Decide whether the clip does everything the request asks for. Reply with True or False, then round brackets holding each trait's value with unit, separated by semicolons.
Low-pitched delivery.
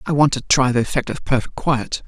True (130 Hz)